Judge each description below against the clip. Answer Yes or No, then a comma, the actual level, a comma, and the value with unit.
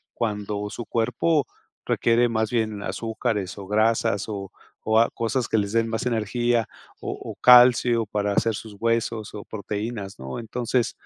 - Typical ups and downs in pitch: No, narrow, 2.3 semitones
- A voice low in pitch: Yes, low, 110 Hz